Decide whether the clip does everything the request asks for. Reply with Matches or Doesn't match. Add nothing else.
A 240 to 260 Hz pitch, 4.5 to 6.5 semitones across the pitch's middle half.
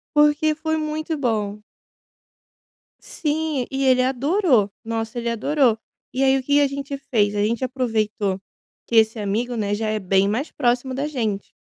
Matches